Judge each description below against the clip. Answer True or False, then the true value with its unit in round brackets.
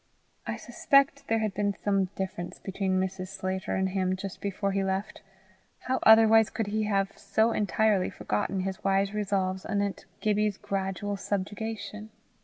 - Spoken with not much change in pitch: True (1.9 semitones)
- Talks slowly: False (150 wpm)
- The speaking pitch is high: True (200 Hz)